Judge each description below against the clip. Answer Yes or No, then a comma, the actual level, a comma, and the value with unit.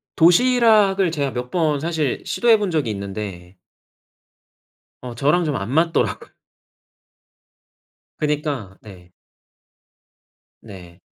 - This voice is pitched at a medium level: Yes, medium, 145 Hz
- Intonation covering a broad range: Yes, wide, 8.7 semitones